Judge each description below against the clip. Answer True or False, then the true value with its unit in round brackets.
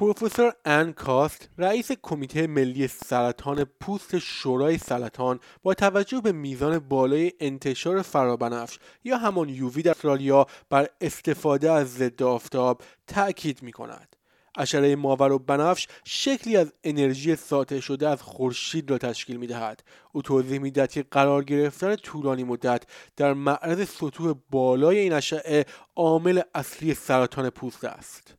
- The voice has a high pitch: False (140 Hz)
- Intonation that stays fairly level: False (3.9 semitones)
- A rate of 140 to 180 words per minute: False (130 wpm)